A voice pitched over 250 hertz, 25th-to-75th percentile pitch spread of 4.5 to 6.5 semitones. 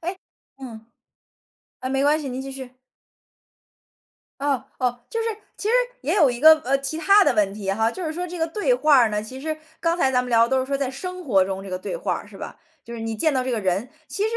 Yes: very high, 265 Hz; wide, 5.5 semitones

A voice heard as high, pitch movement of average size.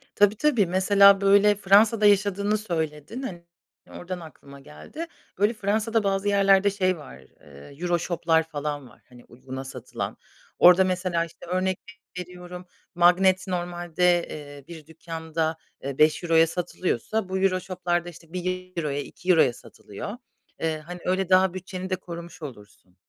No: medium, 180 Hz; average, 3.2 semitones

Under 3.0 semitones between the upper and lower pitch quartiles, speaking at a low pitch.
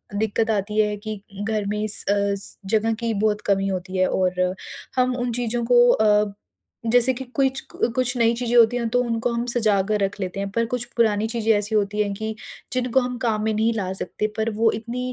No: narrow, 2.6 semitones; high, 220 Hz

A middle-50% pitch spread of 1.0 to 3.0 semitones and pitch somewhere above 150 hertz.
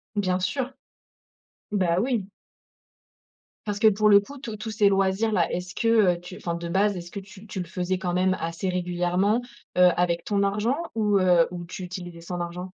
Yes: average, 2.7 semitones; high, 190 Hz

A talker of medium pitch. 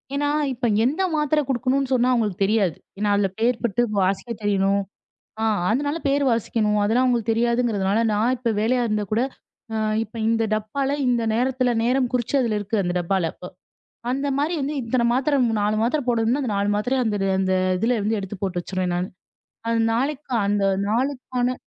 No: high, 230 Hz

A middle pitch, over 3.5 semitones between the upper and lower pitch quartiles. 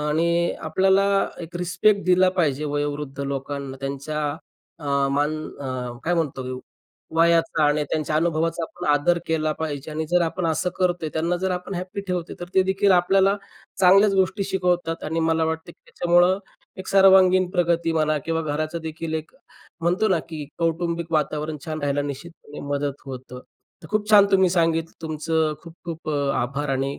No: medium, 165 Hz; average, 3.0 semitones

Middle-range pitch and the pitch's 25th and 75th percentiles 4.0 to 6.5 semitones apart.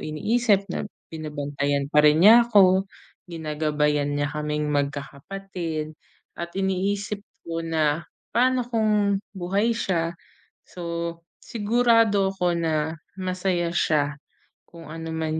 Yes: medium, 170 Hz; average, 4.7 semitones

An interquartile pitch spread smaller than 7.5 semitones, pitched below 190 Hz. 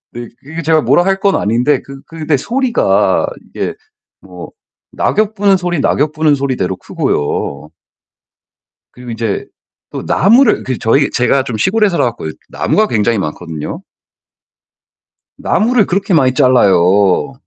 No: wide, 8.9 semitones; medium, 140 Hz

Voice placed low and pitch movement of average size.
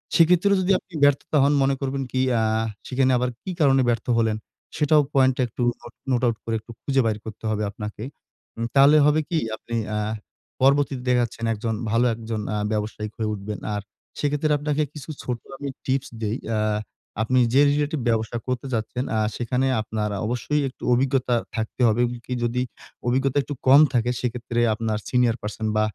Yes: low, 125 Hz; average, 3.6 semitones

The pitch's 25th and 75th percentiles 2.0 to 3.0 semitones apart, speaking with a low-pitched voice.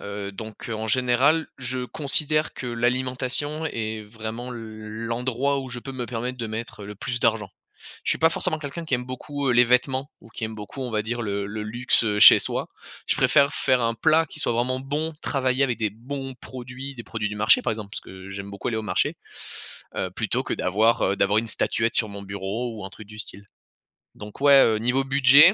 No: average, 3.5 semitones; low, 120 Hz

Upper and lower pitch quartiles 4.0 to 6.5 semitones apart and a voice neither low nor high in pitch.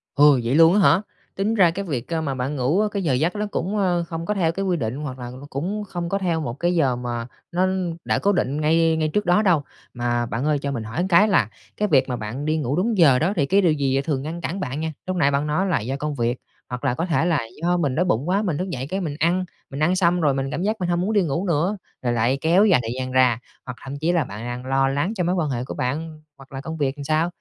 Yes: average, 4.9 semitones; medium, 155 Hz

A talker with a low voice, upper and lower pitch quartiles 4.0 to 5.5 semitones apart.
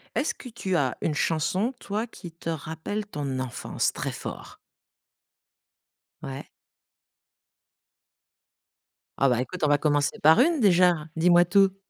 No: medium, 165 Hz; average, 5.1 semitones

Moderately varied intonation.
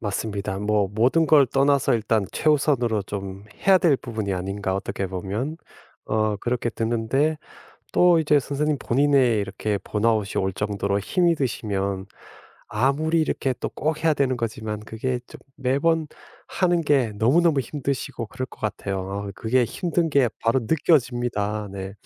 No: wide, 5.7 semitones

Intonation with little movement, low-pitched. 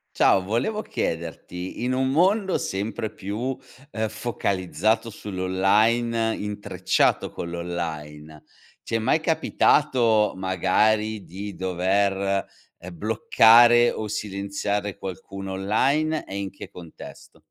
No: average, 3.7 semitones; low, 105 Hz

